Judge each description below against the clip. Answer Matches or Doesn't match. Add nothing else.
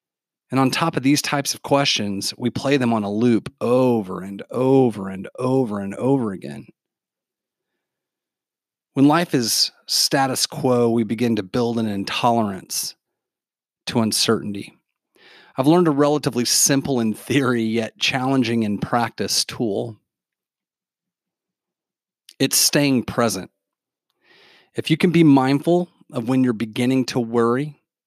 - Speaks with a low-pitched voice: Matches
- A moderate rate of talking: Doesn't match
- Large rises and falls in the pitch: Doesn't match